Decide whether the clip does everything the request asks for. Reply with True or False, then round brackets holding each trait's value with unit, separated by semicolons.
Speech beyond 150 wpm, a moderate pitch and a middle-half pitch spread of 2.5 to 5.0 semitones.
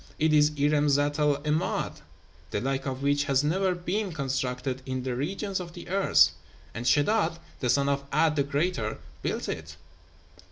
True (170 wpm; 145 Hz; 3.8 semitones)